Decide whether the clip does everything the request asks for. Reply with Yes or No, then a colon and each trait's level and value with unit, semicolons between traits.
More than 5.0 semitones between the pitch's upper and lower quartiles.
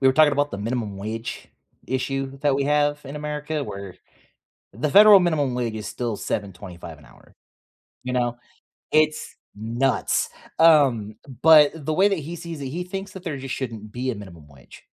Yes: wide, 5.5 semitones